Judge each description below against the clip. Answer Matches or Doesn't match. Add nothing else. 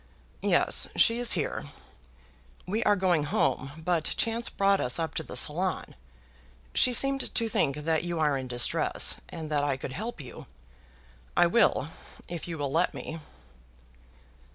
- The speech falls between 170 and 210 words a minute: Doesn't match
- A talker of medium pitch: Matches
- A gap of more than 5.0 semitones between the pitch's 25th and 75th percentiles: Matches